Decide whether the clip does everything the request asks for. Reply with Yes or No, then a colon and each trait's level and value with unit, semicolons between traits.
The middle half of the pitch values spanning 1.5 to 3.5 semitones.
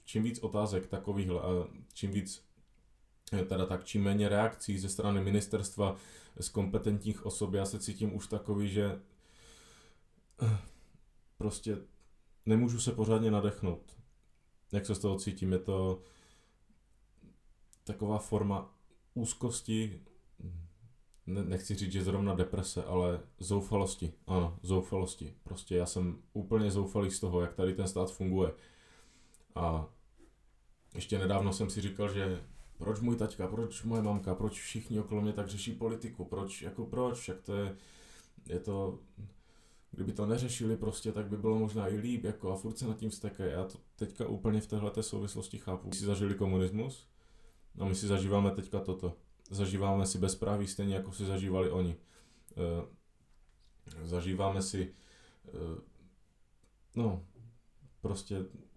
Yes: narrow, 2.4 semitones